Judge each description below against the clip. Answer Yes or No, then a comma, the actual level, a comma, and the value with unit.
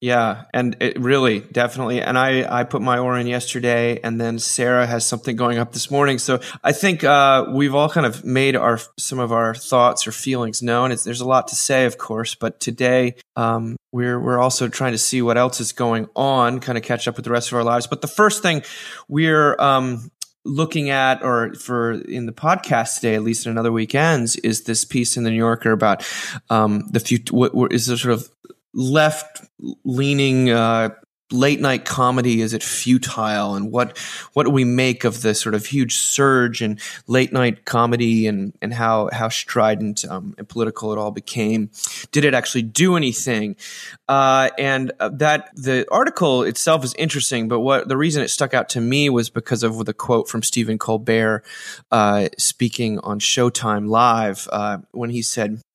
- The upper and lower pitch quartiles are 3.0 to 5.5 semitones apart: No, narrow, 2.5 semitones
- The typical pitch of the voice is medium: No, low, 120 Hz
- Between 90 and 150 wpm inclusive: No, average, 190 wpm